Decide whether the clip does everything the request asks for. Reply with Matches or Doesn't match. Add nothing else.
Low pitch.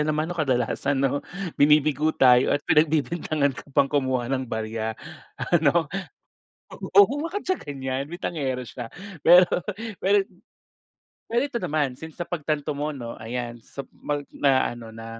Doesn't match